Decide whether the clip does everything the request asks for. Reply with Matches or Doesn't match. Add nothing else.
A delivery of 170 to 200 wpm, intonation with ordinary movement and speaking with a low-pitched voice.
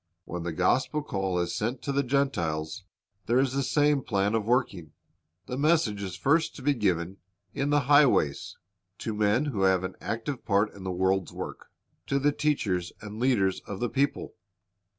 Doesn't match